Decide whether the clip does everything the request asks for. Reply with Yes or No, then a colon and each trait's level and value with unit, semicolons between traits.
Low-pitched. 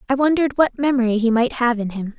No: very high, 250 Hz